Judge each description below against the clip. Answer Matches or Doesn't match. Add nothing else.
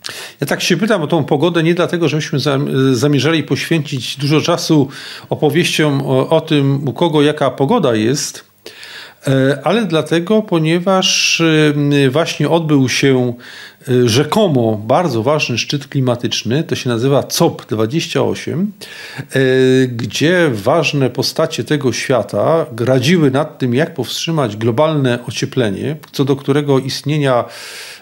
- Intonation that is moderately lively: Matches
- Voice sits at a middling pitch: Matches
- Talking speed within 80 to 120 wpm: Matches